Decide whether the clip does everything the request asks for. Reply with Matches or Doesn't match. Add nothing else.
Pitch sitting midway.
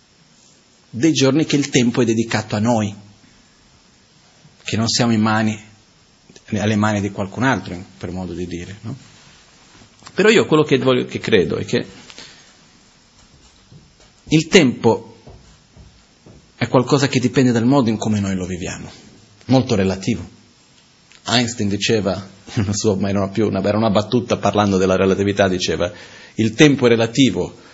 Doesn't match